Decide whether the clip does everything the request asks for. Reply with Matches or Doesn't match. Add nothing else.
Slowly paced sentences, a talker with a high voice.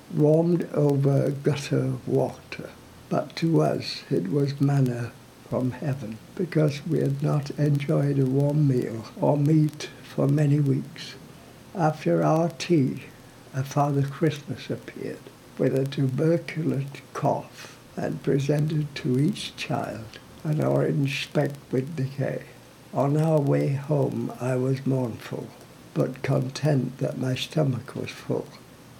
Doesn't match